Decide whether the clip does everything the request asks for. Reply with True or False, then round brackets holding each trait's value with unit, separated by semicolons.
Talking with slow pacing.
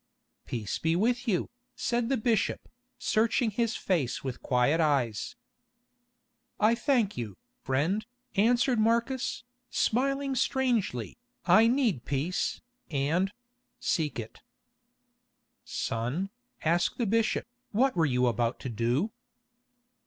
True (110 wpm)